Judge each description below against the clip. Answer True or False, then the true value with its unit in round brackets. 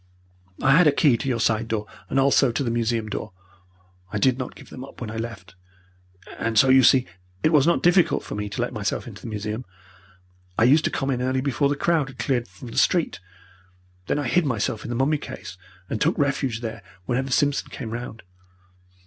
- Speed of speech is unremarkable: False (215 wpm)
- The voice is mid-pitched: False (125 Hz)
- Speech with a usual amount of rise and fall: True (3.5 semitones)